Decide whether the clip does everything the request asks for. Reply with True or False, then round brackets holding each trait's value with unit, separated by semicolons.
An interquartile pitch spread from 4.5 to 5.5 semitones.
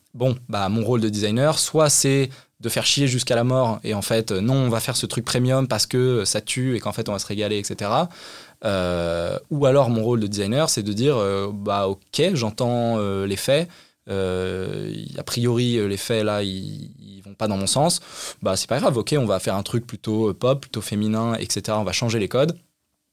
False (4.1 semitones)